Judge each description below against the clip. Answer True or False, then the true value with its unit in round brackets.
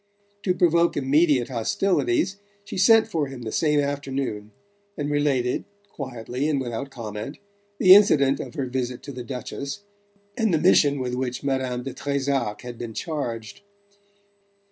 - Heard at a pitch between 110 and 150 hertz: True (140 Hz)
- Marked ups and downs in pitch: False (3.7 semitones)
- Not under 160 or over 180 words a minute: False (145 wpm)